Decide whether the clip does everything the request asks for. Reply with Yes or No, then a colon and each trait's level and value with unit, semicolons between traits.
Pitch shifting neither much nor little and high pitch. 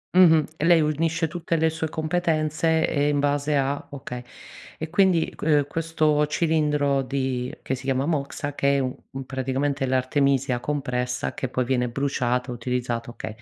No: average, 3.3 semitones; medium, 145 Hz